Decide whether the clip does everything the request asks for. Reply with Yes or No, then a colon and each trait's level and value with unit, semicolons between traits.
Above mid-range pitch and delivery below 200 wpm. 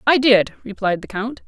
No: high, 225 Hz; fast, 205 wpm